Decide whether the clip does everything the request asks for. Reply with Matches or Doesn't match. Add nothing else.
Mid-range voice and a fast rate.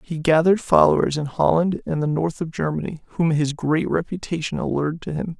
Doesn't match